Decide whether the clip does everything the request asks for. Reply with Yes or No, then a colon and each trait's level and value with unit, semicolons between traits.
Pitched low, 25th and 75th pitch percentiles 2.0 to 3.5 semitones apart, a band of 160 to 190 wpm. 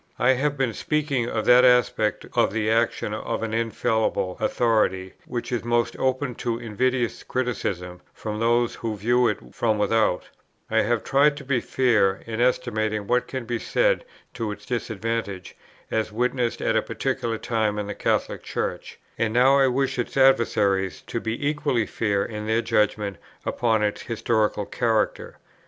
Yes: low, 115 Hz; narrow, 2.6 semitones; average, 165 wpm